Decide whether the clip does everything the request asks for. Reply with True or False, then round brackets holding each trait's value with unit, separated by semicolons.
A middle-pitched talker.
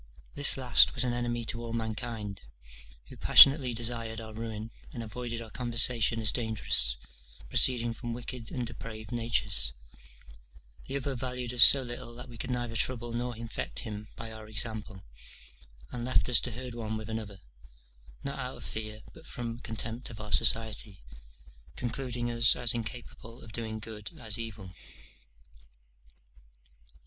False (115 Hz)